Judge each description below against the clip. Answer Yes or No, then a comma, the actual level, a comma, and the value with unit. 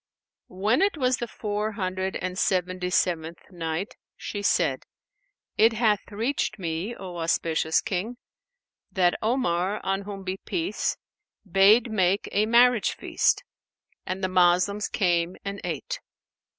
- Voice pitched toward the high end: Yes, high, 195 Hz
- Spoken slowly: Yes, slow, 130 wpm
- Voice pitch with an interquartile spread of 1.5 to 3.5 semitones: Yes, average, 3.2 semitones